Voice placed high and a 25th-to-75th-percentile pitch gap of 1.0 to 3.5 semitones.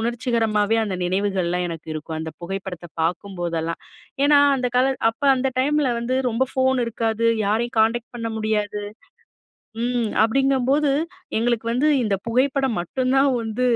No: high, 230 Hz; average, 4.5 semitones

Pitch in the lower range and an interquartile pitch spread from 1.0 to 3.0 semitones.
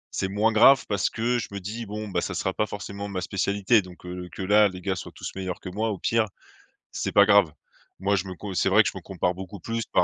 Yes: low, 100 Hz; narrow, 2.4 semitones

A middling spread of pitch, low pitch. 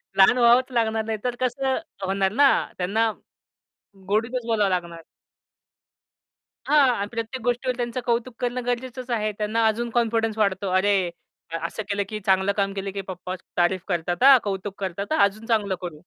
No: average, 3.7 semitones; high, 220 Hz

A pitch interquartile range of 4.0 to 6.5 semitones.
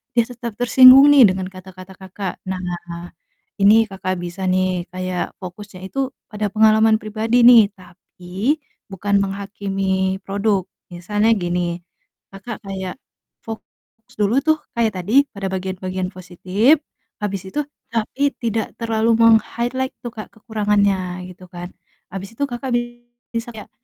No: average, 3.2 semitones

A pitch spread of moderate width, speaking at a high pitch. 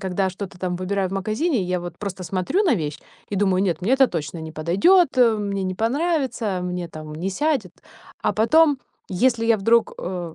Yes: average, 4.7 semitones; high, 195 Hz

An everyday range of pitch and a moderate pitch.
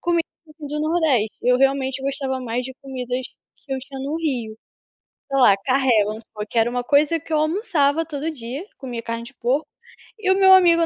No: average, 4.1 semitones; very high, 270 Hz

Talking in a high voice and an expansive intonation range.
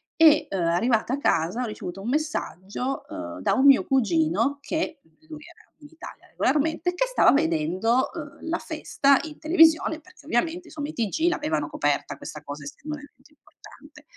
Yes: very high, 275 Hz; wide, 9.0 semitones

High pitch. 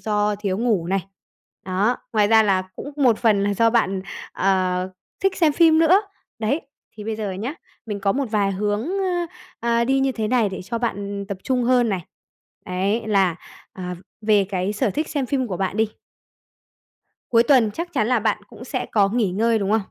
Yes: high, 215 Hz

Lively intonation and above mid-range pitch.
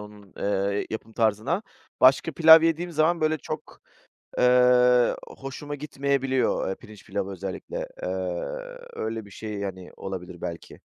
No: wide, 6.4 semitones; low, 125 Hz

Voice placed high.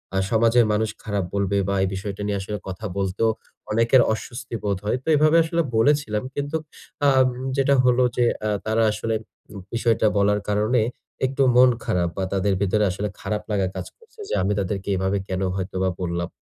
No: low, 105 Hz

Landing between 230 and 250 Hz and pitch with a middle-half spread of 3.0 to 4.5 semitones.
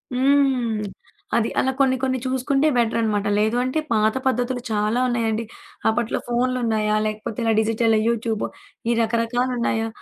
No: high, 235 Hz; narrow, 2.5 semitones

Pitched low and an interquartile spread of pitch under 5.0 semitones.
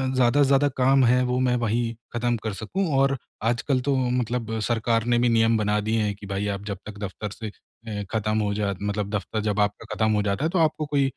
Yes: low, 115 Hz; average, 3.1 semitones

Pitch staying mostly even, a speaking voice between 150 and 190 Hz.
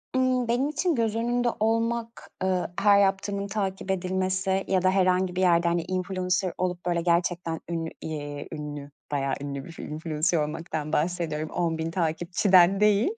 No: average, 3.5 semitones; medium, 185 Hz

